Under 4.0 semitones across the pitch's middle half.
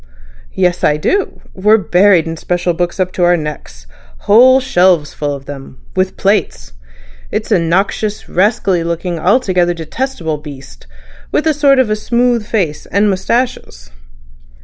No: average, 4.9 semitones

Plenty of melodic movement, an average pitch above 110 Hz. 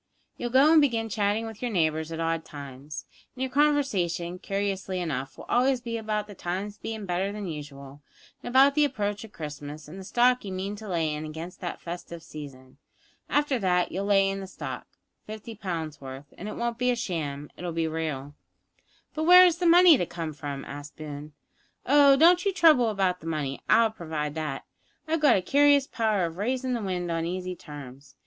Yes: wide, 7.3 semitones; high, 190 Hz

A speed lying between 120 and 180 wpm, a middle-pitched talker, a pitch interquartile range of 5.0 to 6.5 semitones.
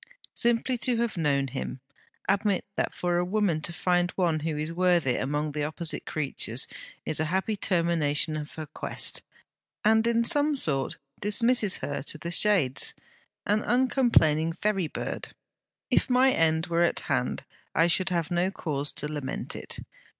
Yes: average, 160 wpm; medium, 170 Hz; wide, 5.5 semitones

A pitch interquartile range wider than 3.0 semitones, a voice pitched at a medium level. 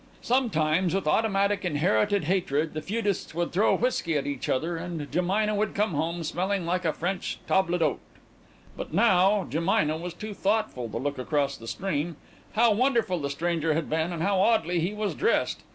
Yes: average, 4.2 semitones; medium, 175 Hz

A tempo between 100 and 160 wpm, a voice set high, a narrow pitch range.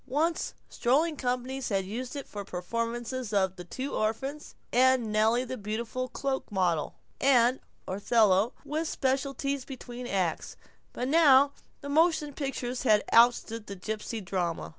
No: average, 140 wpm; high, 245 Hz; average, 4.1 semitones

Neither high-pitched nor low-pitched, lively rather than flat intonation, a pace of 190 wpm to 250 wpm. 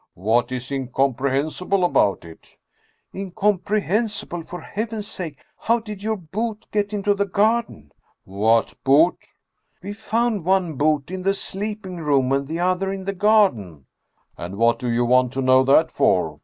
No: medium, 175 Hz; wide, 7.9 semitones; average, 175 wpm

